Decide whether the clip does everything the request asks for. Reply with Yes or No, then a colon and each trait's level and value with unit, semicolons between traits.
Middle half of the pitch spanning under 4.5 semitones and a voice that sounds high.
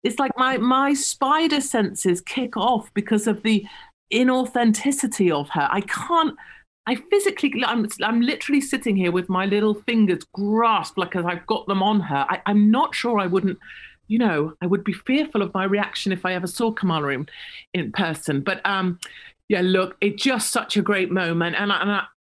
No: average, 5.0 semitones; high, 210 Hz